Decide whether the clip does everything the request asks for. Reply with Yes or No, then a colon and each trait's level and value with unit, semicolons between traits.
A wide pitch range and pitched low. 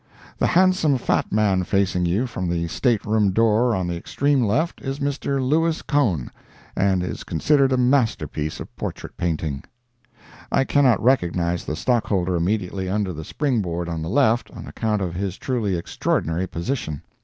Yes: wide, 6.8 semitones; low, 105 Hz